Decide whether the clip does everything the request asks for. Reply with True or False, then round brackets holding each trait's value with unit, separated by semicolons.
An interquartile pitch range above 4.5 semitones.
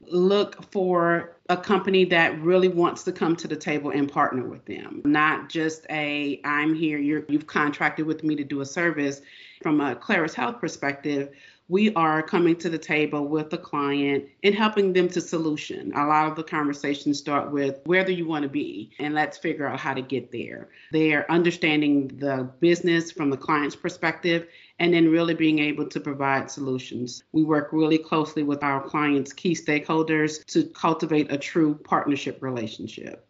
False (2.9 semitones)